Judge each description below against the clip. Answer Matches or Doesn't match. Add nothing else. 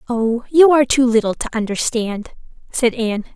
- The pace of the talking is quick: Doesn't match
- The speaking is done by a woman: Matches